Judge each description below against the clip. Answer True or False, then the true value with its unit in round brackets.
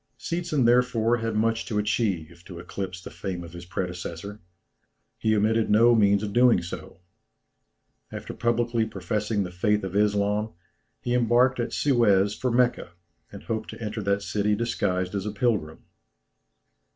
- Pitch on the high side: False (105 Hz)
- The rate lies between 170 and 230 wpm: False (150 wpm)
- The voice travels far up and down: False (3.4 semitones)